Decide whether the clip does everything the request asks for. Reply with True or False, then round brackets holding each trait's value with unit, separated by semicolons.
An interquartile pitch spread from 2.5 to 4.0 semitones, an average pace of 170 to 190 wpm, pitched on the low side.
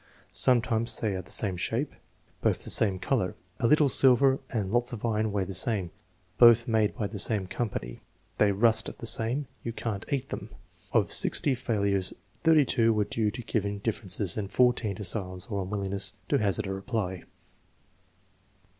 True (3.4 semitones; 175 wpm; 110 Hz)